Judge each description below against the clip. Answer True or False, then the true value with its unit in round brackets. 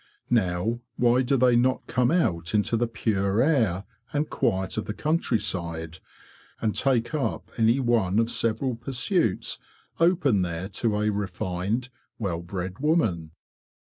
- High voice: False (110 Hz)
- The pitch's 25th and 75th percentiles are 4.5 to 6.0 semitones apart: True (5.2 semitones)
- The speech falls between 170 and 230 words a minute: False (140 wpm)